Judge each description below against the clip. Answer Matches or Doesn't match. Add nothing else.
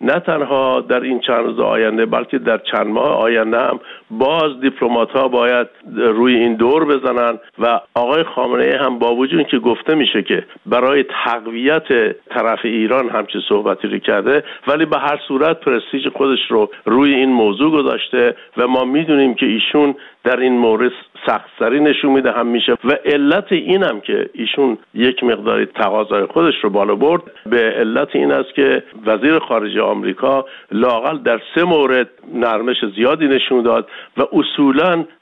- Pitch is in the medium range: Doesn't match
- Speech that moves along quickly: Matches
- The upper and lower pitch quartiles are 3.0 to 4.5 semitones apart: Matches